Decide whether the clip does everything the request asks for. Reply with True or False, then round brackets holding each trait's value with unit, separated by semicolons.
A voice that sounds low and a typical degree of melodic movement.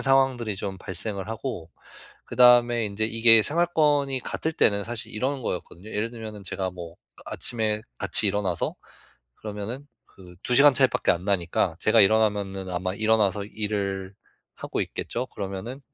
True (110 Hz; 3.9 semitones)